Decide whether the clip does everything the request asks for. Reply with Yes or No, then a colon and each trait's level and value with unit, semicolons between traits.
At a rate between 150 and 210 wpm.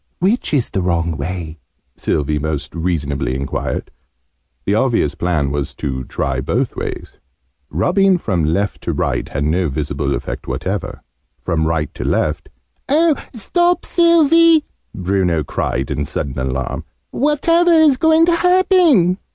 No: slow, 135 wpm